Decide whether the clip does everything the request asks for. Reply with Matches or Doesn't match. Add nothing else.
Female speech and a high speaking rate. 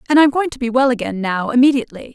Matches